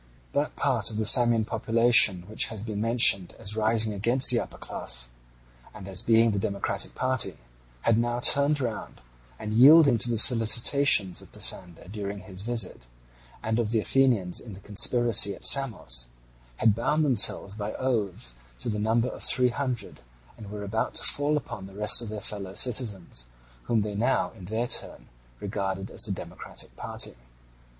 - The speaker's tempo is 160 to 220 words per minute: Yes, average, 170 wpm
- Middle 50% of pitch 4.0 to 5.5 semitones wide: No, average, 3.3 semitones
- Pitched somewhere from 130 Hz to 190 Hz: No, low, 110 Hz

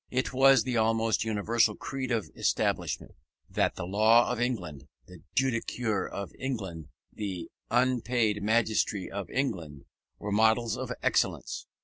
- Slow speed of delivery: Yes, slow, 130 wpm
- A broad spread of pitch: No, average, 3.3 semitones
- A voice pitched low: Yes, low, 110 Hz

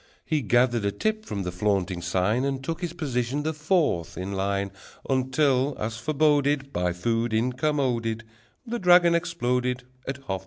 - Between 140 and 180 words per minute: Yes, average, 165 wpm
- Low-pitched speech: Yes, low, 125 Hz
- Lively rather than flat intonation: Yes, wide, 5.9 semitones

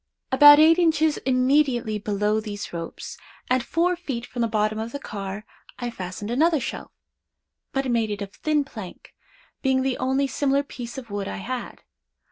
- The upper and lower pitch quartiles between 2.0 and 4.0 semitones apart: No, average, 4.9 semitones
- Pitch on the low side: No, high, 245 Hz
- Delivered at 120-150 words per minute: No, average, 160 wpm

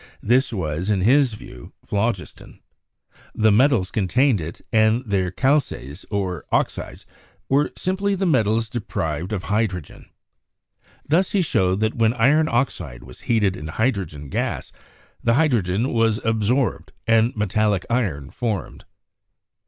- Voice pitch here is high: No, low, 110 Hz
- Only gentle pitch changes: No, average, 5.1 semitones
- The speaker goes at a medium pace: No, slow, 130 wpm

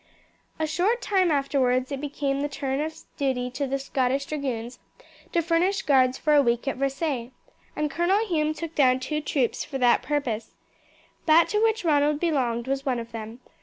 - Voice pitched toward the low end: No, very high, 280 Hz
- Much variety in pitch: No, average, 3.4 semitones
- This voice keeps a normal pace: Yes, average, 180 wpm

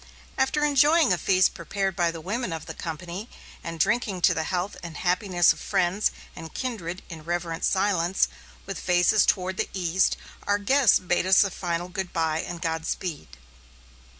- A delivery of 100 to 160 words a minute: No, average, 170 wpm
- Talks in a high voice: No, medium, 180 Hz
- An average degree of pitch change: Yes, average, 3.0 semitones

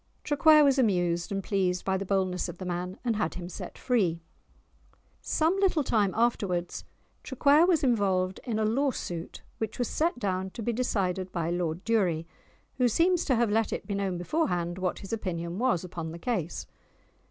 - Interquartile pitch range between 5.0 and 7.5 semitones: Yes, wide, 5.4 semitones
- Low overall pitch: No, high, 195 Hz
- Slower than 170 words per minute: No, average, 185 wpm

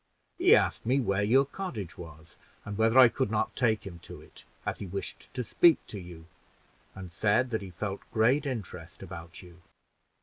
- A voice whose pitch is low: Yes, low, 105 Hz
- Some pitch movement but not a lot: No, wide, 5.7 semitones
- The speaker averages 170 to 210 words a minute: Yes, average, 180 wpm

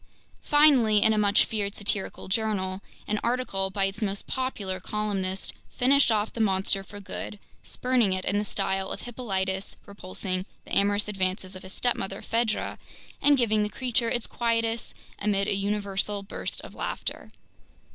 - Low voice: No, high, 205 Hz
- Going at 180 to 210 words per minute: No, average, 155 wpm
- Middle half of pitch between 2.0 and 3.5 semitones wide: Yes, average, 2.9 semitones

